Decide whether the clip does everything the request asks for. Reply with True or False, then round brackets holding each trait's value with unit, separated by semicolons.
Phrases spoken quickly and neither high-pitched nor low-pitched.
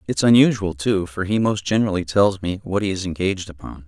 False (215 wpm; 95 Hz)